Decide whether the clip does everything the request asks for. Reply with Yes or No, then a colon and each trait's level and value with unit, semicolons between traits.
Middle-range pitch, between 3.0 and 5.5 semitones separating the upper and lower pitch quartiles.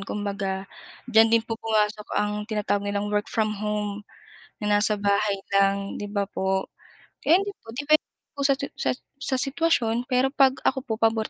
No: high, 215 Hz; average, 3.4 semitones